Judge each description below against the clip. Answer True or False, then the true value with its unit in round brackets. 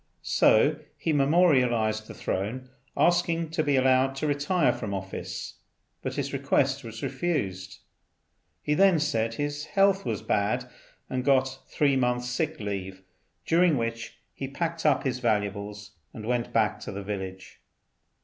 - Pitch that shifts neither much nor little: False (6.0 semitones)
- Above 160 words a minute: False (145 wpm)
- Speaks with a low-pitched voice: True (130 Hz)